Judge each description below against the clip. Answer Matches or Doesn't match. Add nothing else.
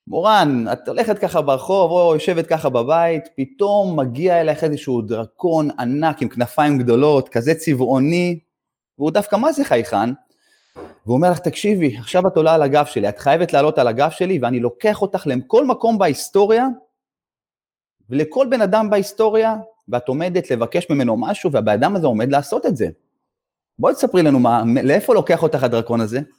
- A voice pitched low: Doesn't match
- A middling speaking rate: Doesn't match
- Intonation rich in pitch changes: Matches